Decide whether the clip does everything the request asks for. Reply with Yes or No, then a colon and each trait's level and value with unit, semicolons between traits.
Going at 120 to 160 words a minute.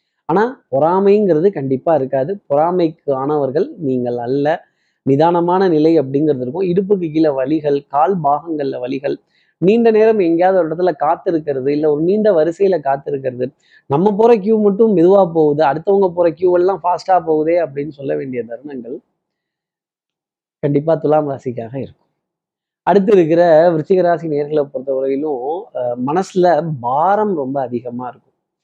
Yes: average, 125 wpm